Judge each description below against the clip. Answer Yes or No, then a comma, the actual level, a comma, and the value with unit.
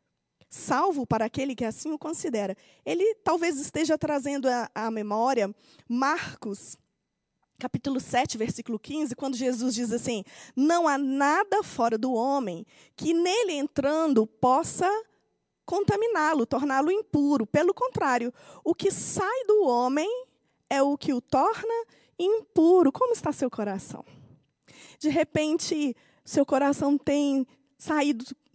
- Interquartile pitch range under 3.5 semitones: No, average, 5.2 semitones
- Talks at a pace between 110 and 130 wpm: Yes, slow, 120 wpm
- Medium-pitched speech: No, very high, 280 Hz